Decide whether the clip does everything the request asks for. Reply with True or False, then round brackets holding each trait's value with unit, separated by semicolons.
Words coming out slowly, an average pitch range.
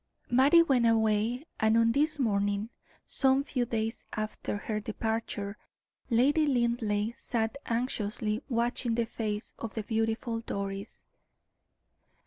False (115 wpm; 2.3 semitones)